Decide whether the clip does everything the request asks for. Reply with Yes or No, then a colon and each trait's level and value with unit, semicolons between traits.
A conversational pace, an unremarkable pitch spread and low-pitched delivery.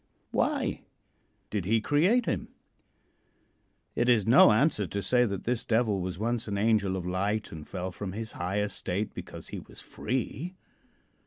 Yes: average, 160 wpm; average, 3.9 semitones; low, 105 Hz